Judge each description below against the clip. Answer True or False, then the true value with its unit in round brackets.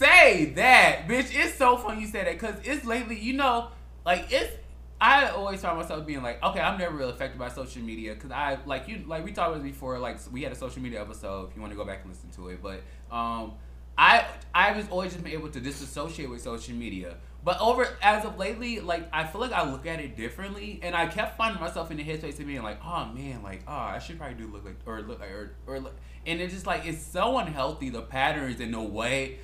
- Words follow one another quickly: True (255 wpm)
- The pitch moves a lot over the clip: True (8.8 semitones)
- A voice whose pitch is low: False (150 Hz)